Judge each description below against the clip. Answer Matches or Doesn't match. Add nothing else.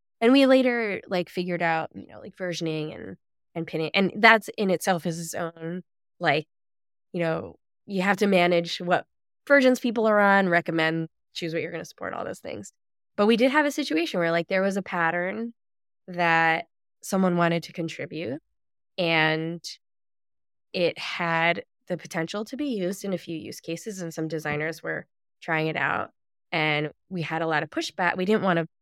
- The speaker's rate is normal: Matches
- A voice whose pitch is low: Doesn't match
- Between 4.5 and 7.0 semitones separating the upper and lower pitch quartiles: Doesn't match